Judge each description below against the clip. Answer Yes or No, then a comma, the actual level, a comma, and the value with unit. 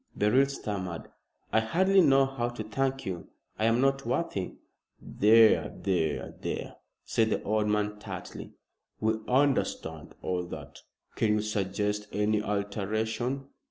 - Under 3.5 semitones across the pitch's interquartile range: No, average, 4.2 semitones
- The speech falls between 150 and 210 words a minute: No, slow, 135 wpm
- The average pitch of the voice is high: No, low, 110 Hz